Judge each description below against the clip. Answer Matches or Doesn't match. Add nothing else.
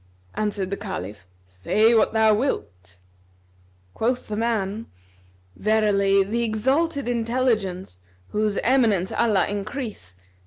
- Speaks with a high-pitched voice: Matches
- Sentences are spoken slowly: Matches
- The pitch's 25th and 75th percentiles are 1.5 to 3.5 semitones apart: Matches